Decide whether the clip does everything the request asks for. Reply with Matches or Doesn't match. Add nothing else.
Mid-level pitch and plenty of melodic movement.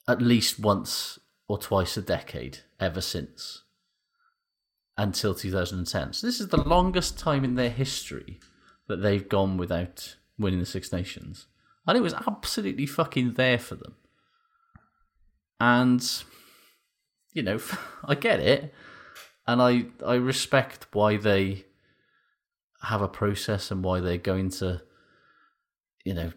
Doesn't match